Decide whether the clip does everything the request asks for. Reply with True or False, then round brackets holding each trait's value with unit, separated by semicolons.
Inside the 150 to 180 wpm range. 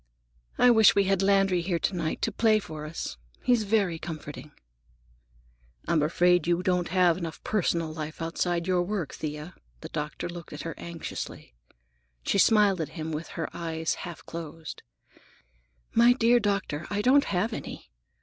True (160 wpm)